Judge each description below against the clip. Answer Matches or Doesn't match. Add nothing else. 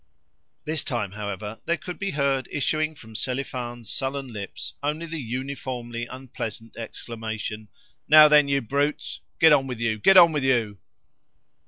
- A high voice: Doesn't match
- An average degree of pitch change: Matches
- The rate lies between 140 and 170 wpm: Matches